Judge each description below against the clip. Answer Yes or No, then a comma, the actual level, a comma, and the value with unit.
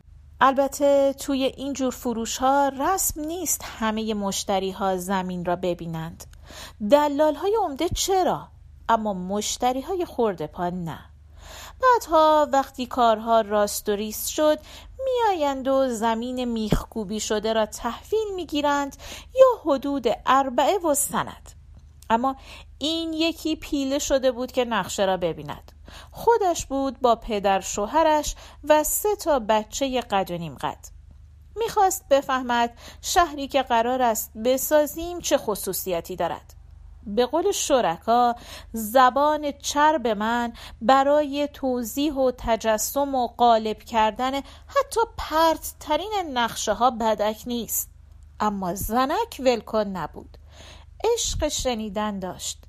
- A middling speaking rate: Yes, average, 120 wpm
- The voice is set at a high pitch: Yes, very high, 250 Hz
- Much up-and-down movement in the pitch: Yes, wide, 5.7 semitones